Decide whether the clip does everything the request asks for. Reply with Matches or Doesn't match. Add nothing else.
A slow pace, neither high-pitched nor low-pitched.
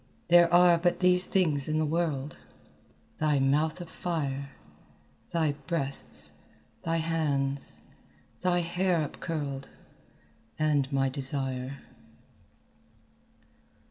Matches